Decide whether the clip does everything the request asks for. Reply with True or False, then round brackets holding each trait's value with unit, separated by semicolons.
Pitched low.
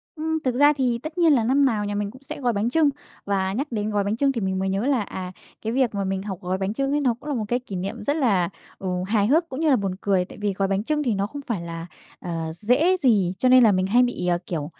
False (220 Hz)